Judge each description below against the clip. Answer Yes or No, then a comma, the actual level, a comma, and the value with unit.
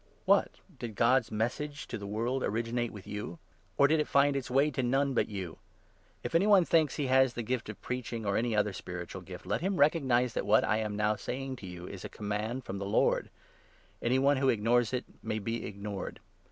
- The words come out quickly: Yes, fast, 235 wpm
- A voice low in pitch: Yes, low, 120 Hz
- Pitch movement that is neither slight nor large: Yes, average, 4.1 semitones